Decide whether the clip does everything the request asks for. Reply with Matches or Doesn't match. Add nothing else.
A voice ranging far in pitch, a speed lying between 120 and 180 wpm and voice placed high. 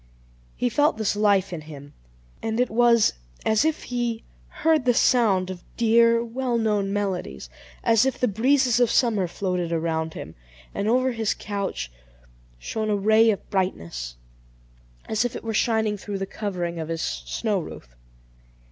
Doesn't match